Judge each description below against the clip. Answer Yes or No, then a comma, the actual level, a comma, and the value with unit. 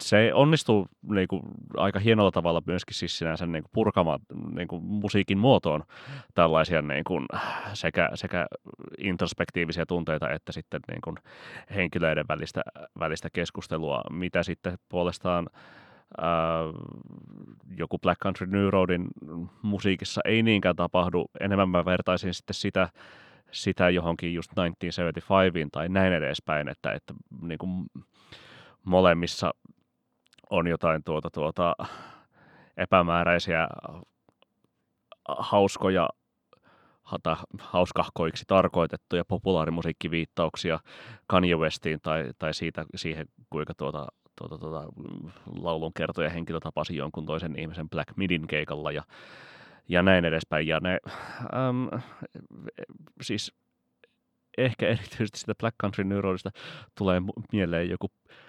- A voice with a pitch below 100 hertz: Yes, very low, 90 Hz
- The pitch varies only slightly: No, average, 3.1 semitones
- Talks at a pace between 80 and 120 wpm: Yes, average, 105 wpm